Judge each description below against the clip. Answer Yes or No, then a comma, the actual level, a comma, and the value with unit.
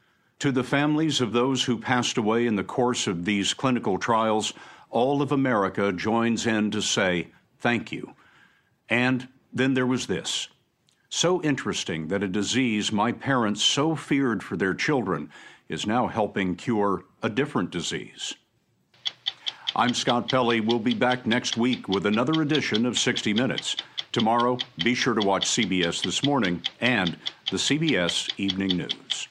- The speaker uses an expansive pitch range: No, average, 3.8 semitones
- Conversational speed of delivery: Yes, average, 155 wpm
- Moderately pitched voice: No, low, 120 Hz